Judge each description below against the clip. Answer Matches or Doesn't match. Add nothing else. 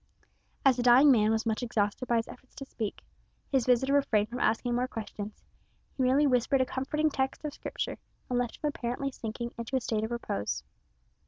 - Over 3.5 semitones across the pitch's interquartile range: Doesn't match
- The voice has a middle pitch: Doesn't match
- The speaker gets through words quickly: Doesn't match